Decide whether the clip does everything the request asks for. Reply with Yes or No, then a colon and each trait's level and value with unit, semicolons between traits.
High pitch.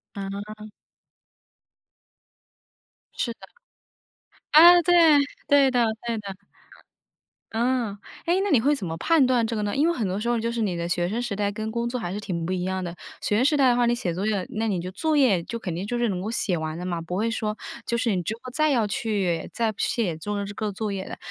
Yes: high, 215 Hz